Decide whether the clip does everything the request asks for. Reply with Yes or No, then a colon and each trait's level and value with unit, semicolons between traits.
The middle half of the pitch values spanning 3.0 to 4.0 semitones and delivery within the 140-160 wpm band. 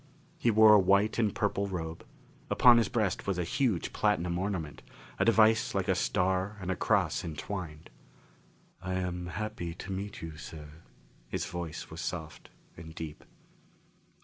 Yes: average, 3.7 semitones; average, 150 wpm